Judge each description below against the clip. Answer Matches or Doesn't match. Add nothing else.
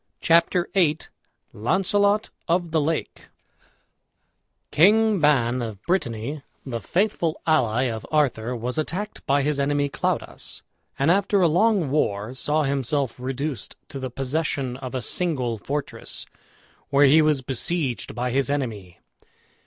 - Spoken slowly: Matches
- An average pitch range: Matches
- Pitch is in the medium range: Matches